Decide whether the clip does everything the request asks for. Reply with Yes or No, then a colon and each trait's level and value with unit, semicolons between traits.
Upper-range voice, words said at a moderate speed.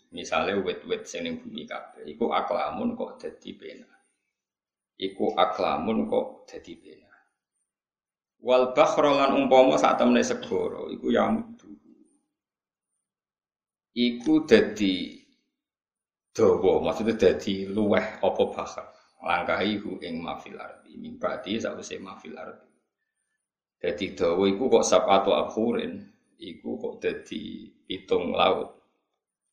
Yes: very high, 270 Hz; average, 110 wpm